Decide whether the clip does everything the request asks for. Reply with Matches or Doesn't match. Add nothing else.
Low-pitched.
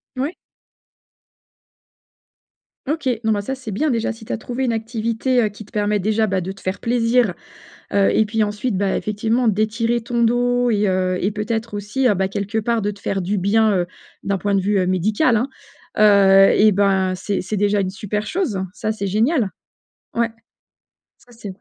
Doesn't match